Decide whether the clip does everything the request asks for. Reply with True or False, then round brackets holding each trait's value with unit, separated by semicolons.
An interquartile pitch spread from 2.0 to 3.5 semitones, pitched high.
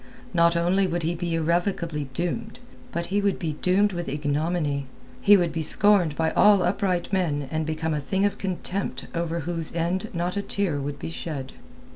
False (3.0 semitones; 170 Hz)